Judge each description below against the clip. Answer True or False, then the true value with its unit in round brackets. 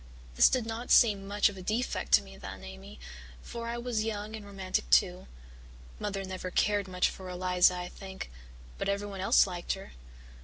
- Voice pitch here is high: True (195 Hz)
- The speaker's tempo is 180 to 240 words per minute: True (185 wpm)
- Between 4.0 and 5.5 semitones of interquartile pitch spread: False (2.5 semitones)